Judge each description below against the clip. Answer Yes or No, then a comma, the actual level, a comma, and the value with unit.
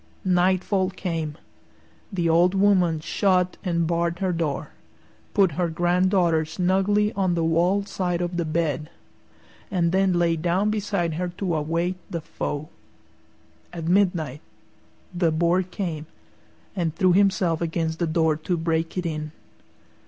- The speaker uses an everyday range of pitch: No, narrow, 2.3 semitones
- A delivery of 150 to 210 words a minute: No, average, 140 wpm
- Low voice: No, medium, 175 Hz